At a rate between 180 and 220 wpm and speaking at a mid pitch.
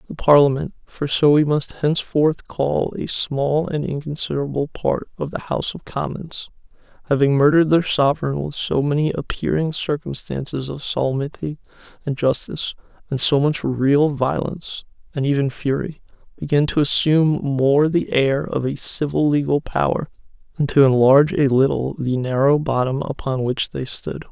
No: average, 150 wpm; medium, 145 Hz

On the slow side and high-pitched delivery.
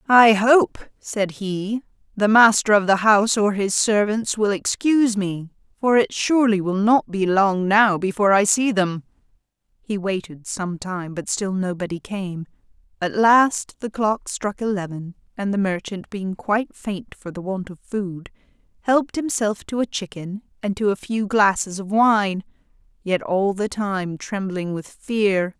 No: average, 165 wpm; high, 200 Hz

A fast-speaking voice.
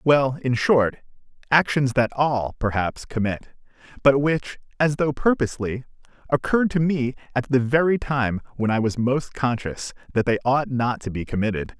No: average, 165 wpm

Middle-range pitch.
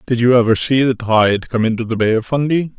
No: low, 120 Hz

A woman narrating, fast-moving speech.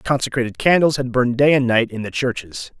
No: male; fast, 215 wpm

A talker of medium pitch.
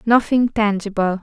No: high, 215 Hz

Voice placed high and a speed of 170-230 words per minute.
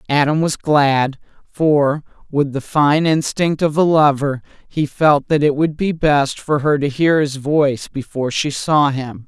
No: medium, 145 Hz; average, 180 wpm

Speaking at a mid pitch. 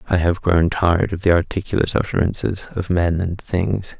No: very low, 90 Hz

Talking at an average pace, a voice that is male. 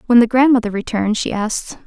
No: average, 195 wpm; female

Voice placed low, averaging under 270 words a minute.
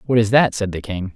No: low, 105 Hz; fast, 310 wpm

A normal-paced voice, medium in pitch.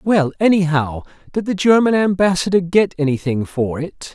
Yes: average, 145 wpm; medium, 170 Hz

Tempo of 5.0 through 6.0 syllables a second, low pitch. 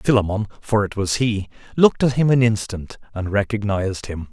Yes: 5.4 syllables/s; low, 105 Hz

